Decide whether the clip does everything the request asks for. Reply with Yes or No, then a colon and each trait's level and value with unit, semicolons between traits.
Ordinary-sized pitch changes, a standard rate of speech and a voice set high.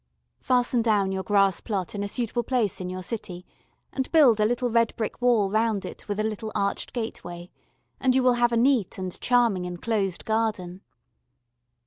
Yes: average, 3.8 semitones; average, 180 wpm; high, 220 Hz